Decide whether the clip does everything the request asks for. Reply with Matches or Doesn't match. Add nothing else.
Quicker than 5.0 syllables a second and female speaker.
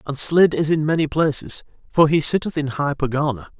Doesn't match